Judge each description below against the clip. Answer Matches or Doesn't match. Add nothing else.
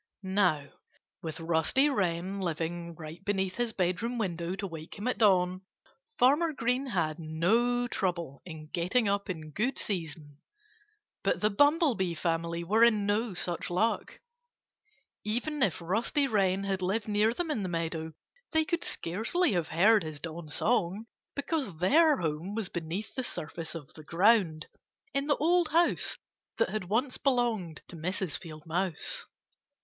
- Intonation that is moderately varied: Doesn't match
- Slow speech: Doesn't match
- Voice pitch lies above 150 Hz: Matches